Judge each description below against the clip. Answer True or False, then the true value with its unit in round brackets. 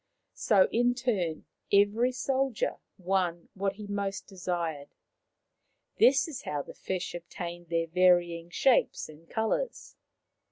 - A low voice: False (190 Hz)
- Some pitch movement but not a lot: True (4.5 semitones)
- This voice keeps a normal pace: False (120 wpm)